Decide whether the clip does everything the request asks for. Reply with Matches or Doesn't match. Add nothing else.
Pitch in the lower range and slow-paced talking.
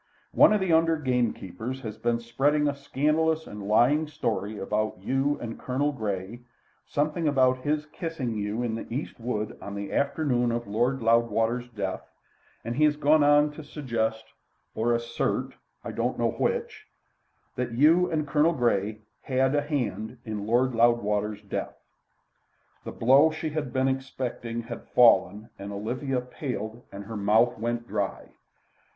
Doesn't match